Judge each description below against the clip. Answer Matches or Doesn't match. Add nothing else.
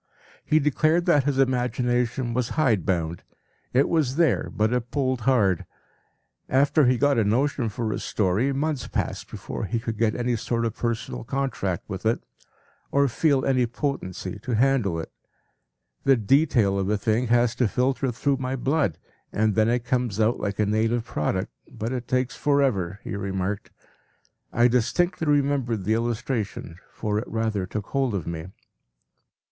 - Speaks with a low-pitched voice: Matches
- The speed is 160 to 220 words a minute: Matches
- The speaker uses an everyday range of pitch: Matches